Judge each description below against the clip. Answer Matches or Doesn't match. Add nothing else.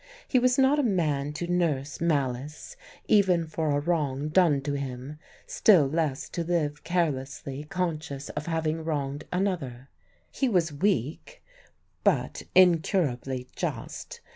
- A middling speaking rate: Doesn't match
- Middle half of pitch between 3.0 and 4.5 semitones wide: Matches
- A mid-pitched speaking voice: Matches